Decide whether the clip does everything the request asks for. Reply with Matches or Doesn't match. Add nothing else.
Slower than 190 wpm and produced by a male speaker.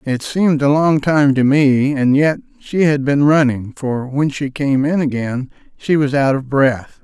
Doesn't match